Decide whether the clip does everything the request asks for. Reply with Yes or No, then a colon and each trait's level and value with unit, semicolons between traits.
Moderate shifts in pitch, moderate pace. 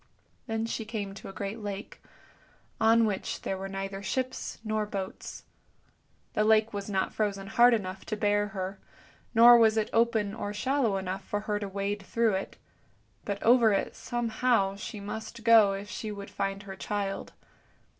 No: narrow, 2.2 semitones; average, 170 wpm